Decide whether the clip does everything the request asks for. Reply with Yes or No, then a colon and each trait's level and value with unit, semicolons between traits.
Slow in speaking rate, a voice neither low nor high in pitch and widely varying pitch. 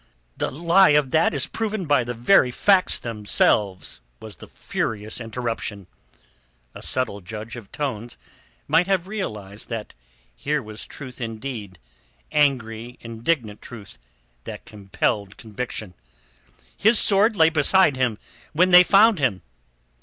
No: slow, 130 wpm; low, 125 Hz; wide, 7.1 semitones